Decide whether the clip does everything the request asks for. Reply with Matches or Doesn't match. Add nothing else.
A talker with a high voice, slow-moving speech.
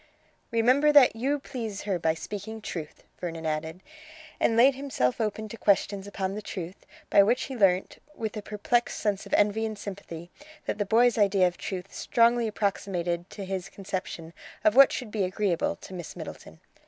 Doesn't match